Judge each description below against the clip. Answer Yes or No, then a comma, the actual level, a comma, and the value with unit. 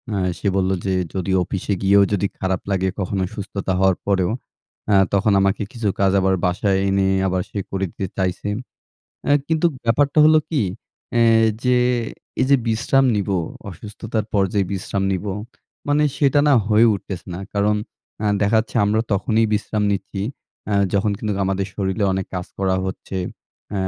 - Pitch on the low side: Yes, low, 100 Hz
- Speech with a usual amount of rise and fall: No, narrow, 2.2 semitones